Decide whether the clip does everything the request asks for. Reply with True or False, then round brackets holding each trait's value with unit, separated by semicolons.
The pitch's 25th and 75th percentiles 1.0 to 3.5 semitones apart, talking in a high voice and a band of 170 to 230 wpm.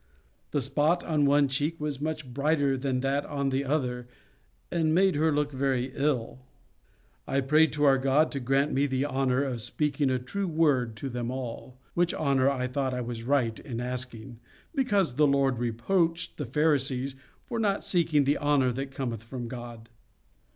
False (2.9 semitones; 135 Hz; 180 wpm)